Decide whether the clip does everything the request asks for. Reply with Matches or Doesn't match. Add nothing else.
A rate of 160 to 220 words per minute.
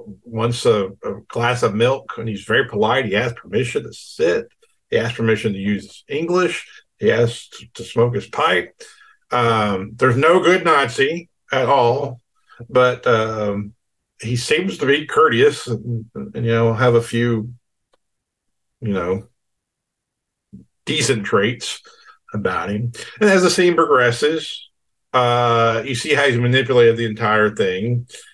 Doesn't match